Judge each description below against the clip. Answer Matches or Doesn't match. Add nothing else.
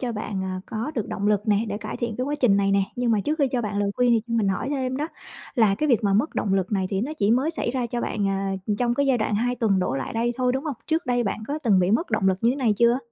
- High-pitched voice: Matches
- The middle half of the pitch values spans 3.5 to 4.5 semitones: Matches